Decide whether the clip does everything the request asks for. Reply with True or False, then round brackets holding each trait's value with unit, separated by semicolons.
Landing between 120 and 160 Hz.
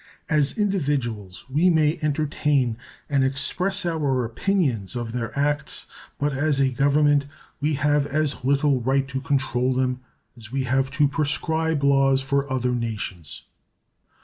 True (140 Hz)